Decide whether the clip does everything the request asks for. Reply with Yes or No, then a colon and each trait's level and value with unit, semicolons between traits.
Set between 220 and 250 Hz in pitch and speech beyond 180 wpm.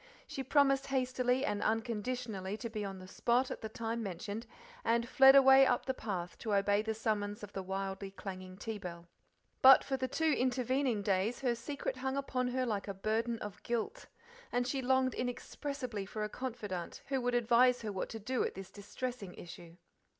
Yes: high, 230 Hz; average, 190 wpm